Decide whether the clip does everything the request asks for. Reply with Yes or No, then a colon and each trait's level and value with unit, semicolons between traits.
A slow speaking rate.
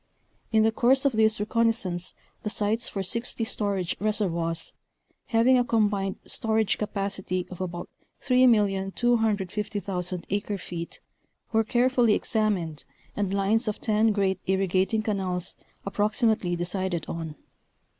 Yes: slow, 115 wpm